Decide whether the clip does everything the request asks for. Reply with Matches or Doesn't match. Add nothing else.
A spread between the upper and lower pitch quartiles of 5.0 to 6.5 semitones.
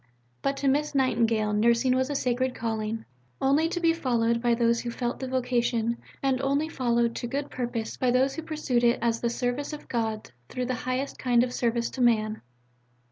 Doesn't match